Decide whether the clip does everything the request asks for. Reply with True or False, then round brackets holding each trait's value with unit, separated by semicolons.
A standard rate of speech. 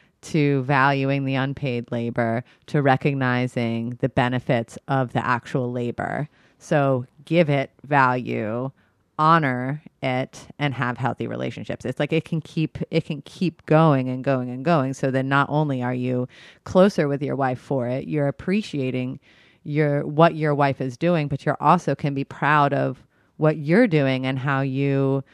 True (165 wpm)